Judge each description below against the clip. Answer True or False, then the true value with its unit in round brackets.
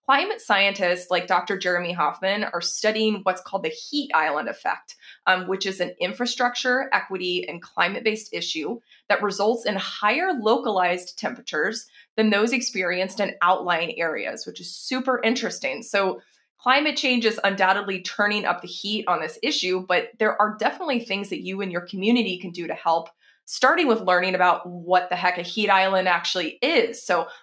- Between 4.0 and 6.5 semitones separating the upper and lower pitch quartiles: True (4.3 semitones)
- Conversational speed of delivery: True (175 wpm)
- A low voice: False (200 Hz)